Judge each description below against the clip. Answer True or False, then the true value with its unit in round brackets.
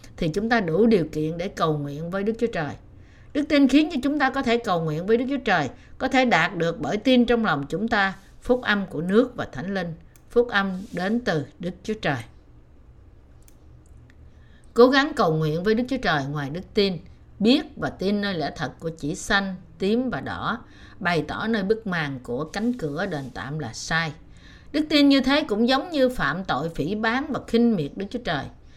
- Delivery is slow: False (215 wpm)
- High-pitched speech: True (195 Hz)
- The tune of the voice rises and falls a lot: True (7.5 semitones)